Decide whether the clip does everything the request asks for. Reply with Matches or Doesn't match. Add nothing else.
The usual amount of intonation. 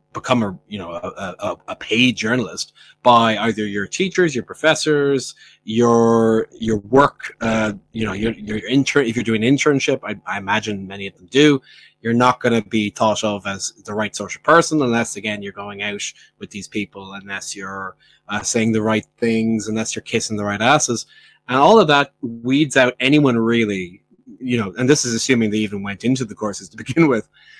Matches